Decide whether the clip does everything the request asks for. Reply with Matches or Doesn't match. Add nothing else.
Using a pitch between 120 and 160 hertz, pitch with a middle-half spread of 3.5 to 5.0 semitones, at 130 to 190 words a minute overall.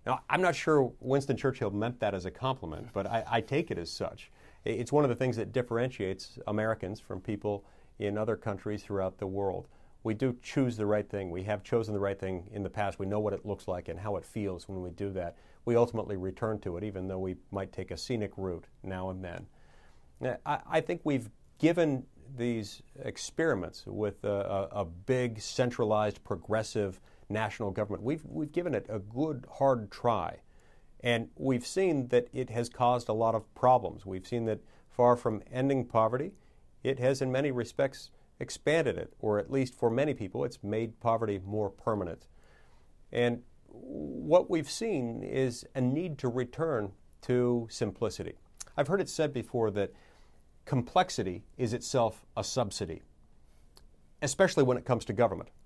Doesn't match